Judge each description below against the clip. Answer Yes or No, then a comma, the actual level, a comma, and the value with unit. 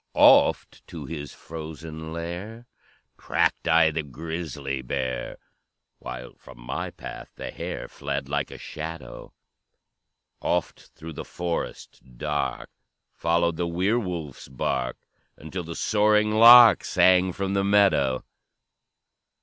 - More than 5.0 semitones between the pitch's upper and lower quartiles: No, average, 4.4 semitones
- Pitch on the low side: Yes, very low, 80 Hz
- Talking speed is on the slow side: Yes, slow, 115 wpm